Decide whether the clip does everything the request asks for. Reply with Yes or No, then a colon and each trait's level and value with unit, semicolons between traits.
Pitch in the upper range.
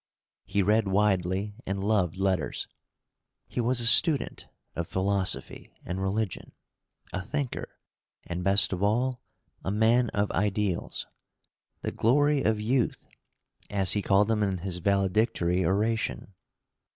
No: low, 100 Hz